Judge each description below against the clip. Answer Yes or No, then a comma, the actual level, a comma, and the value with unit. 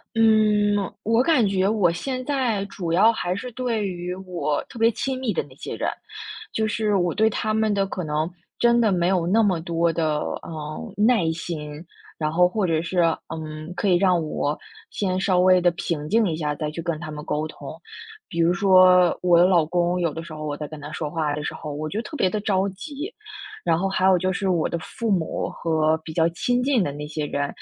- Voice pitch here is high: No, medium, 180 Hz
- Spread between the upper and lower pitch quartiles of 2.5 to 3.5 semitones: No, average, 4.6 semitones